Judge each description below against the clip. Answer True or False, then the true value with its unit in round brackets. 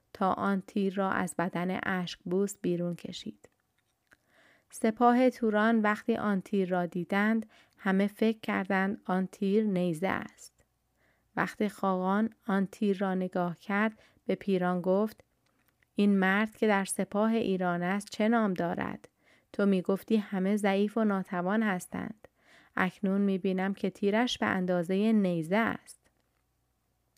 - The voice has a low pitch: False (195 Hz)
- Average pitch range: False (2.3 semitones)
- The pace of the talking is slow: False (135 wpm)